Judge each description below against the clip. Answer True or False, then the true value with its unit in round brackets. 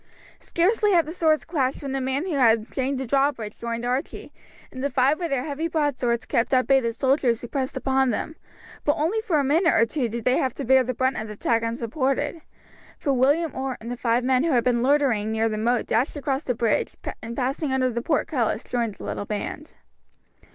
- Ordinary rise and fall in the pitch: True (3.5 semitones)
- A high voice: True (260 Hz)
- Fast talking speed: True (225 wpm)